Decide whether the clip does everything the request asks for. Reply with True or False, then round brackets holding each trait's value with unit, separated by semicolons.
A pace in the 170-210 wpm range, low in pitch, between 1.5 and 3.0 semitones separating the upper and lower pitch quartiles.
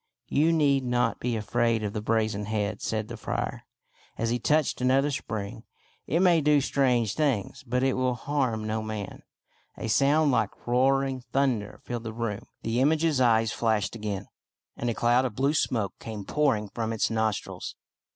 False (180 wpm; 120 Hz; 3.9 semitones)